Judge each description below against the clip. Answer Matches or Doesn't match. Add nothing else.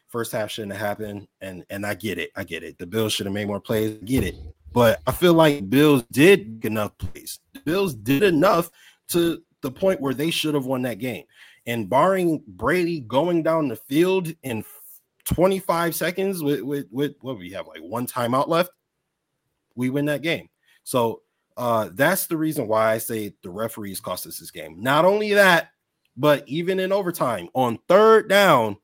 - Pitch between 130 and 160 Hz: Matches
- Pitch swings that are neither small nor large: Doesn't match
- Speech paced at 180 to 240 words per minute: Matches